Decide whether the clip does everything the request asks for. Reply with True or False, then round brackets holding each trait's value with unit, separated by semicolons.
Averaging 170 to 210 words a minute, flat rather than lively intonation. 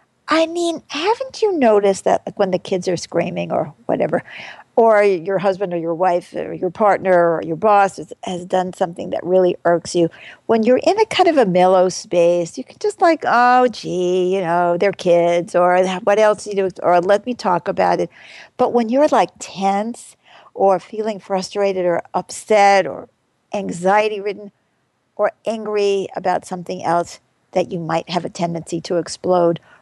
False (185 wpm; 3.5 semitones)